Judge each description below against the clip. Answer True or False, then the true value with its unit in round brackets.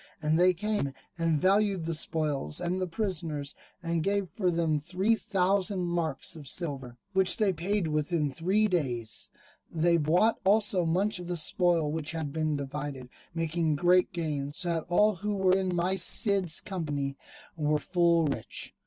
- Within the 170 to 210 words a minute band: False (160 wpm)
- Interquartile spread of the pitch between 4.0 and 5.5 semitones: False (3.6 semitones)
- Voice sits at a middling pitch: True (170 Hz)